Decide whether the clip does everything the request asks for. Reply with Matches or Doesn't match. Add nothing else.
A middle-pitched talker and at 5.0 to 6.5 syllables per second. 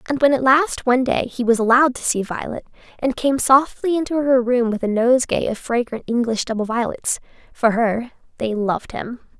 Doesn't match